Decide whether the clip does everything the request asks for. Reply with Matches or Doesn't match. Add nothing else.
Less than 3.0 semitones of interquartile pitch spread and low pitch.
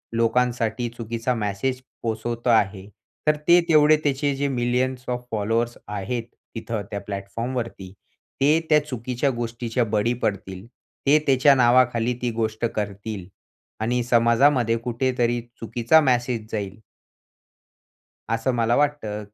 Matches